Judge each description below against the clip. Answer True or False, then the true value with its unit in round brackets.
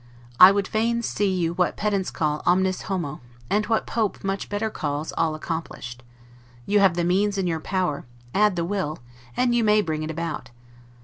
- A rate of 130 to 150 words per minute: False (185 wpm)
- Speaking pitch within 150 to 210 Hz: True (185 Hz)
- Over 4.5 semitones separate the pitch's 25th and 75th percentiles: False (4.1 semitones)